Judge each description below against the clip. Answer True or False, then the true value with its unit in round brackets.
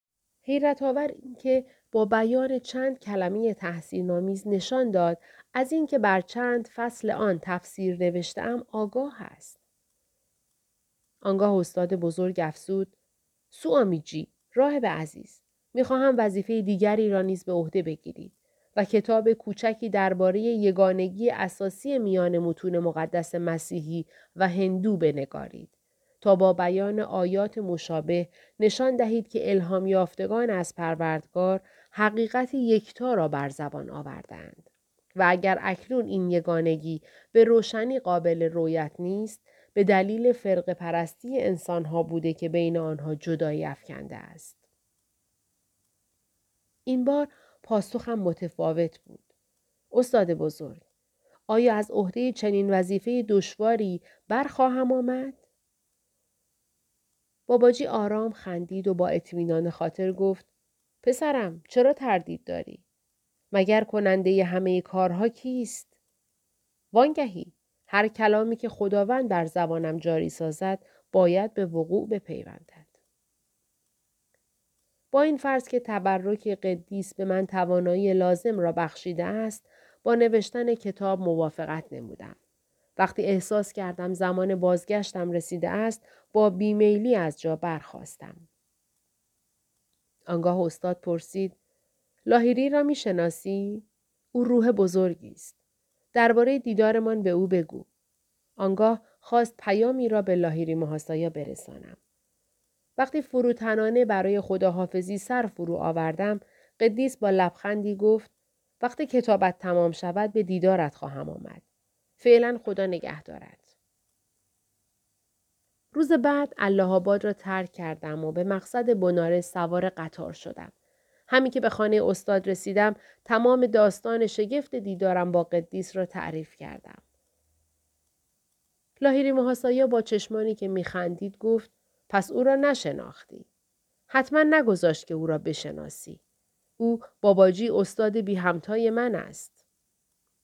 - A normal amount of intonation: True (4.6 semitones)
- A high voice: True (195 Hz)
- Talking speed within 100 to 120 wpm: True (115 wpm)